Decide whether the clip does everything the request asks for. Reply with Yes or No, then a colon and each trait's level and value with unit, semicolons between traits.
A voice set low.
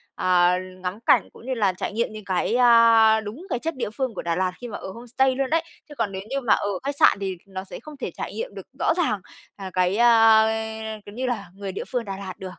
No: high, 220 Hz